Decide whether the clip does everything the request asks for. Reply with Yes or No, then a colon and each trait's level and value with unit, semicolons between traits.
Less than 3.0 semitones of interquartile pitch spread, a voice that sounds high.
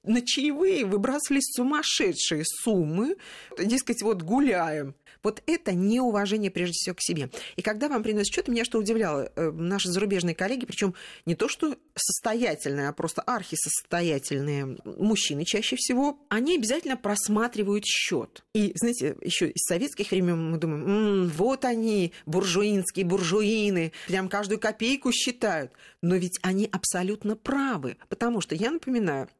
No: average, 5.2 semitones; high, 210 Hz